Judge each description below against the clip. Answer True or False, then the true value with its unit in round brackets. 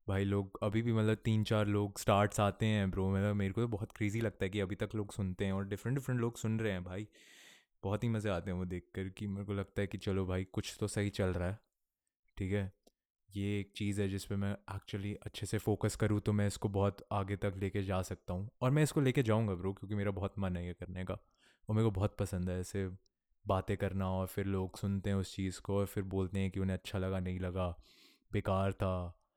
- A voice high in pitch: False (100 Hz)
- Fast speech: True (255 wpm)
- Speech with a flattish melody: True (1.8 semitones)